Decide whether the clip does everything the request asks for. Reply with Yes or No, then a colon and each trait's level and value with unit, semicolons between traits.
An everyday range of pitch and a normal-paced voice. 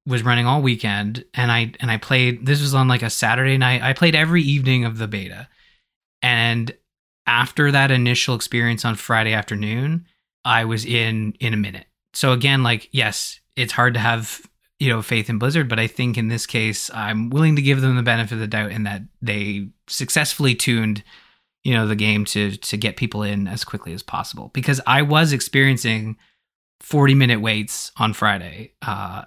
Yes: average, 3.2 semitones; average, 195 wpm